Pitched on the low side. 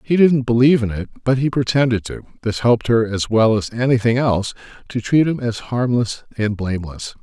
Yes: low, 120 Hz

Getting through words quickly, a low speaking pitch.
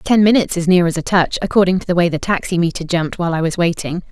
No: fast, 260 wpm; medium, 175 Hz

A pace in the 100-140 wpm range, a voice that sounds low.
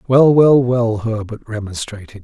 Yes: slow, 135 wpm; low, 115 Hz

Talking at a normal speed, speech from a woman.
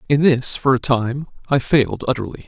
No: average, 195 wpm; male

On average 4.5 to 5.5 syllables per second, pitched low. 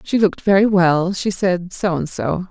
No: 4.6 syllables/s; medium, 185 Hz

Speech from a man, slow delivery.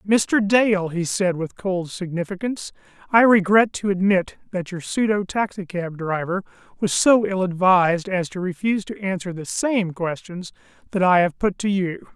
No: male; average, 170 wpm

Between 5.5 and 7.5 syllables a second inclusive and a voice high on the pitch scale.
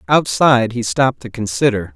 No: 5.6 syllables/s; low, 115 Hz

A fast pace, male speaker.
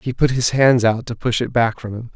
Yes: fast, 305 wpm; male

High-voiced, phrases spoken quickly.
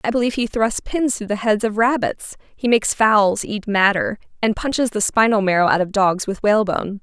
Yes: high, 210 Hz; fast, 215 wpm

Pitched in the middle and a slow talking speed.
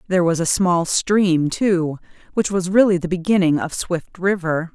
No: medium, 180 Hz; average, 175 wpm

